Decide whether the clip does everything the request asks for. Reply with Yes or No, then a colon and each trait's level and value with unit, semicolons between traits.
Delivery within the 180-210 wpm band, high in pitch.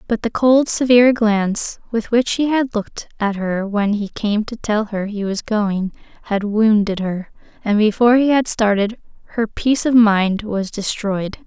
Yes: average, 185 wpm; high, 215 Hz